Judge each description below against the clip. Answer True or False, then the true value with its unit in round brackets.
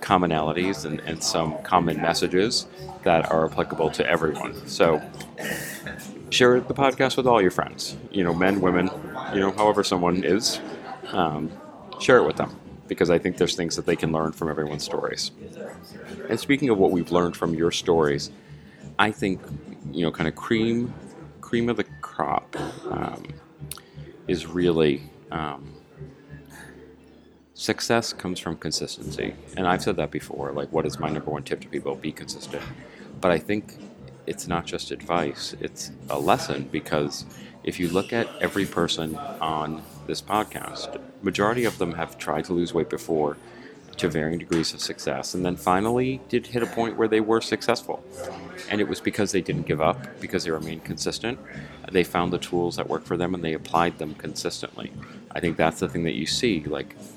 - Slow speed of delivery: False (175 wpm)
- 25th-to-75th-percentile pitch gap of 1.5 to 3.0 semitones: False (4.9 semitones)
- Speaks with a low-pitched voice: True (90 Hz)